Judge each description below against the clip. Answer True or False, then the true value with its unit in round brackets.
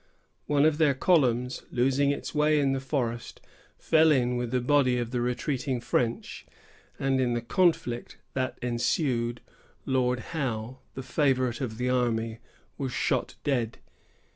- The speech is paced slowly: False (145 wpm)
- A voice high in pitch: False (125 Hz)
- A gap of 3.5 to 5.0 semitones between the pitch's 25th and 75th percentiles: False (2.6 semitones)